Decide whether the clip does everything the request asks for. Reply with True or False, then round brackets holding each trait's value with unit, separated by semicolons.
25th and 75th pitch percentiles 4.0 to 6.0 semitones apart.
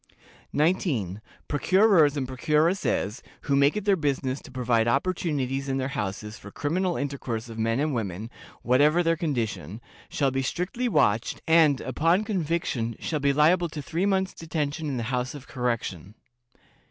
True (5.2 semitones)